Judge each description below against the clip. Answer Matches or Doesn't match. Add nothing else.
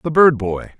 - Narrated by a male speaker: Matches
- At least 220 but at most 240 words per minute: Matches